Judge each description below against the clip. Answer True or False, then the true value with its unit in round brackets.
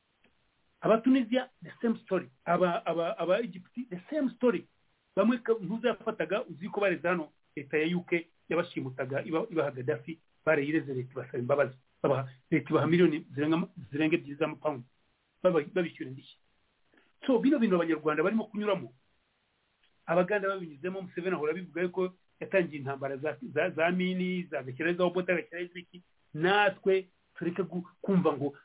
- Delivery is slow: True (125 wpm)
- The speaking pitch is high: False (170 Hz)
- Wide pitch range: False (3.8 semitones)